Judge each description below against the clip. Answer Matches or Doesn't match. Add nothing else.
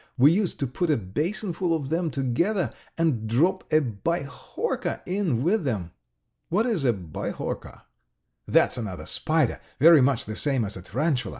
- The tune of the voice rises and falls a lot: Matches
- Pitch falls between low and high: Matches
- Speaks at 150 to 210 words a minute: Matches